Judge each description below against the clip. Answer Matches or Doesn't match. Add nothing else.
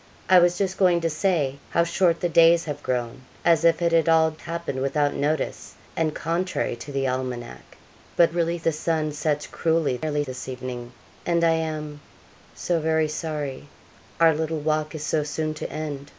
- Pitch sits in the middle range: Matches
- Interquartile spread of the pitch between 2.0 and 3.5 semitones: Matches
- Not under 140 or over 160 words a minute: Doesn't match